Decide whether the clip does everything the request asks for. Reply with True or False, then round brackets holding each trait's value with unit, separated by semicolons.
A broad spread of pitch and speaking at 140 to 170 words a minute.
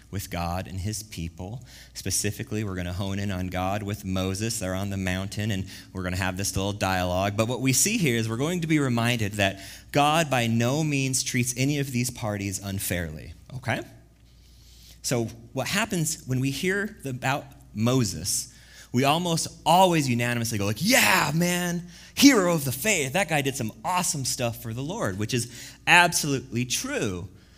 False (6.1 semitones; 180 wpm)